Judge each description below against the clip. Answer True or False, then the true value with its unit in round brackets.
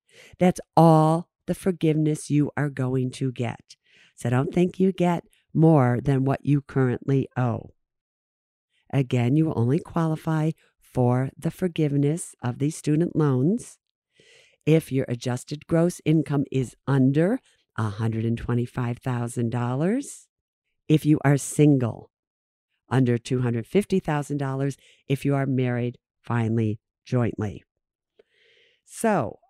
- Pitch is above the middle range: False (140 Hz)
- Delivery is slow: True (110 wpm)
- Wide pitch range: False (4.5 semitones)